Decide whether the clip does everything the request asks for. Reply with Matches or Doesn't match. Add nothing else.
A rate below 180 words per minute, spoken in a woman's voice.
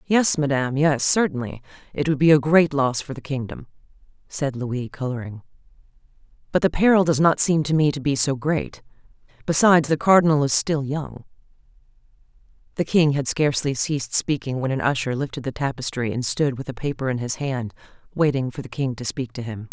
Doesn't match